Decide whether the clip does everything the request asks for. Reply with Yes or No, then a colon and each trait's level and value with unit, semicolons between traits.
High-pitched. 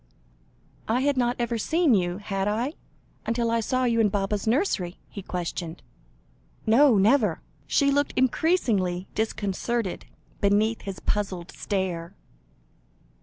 Yes: high, 215 Hz